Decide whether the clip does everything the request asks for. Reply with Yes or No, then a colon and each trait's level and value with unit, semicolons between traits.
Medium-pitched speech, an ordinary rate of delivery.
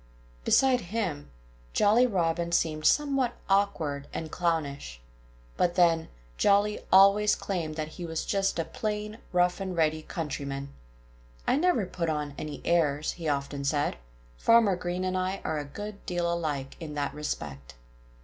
Yes: medium, 170 Hz; average, 150 wpm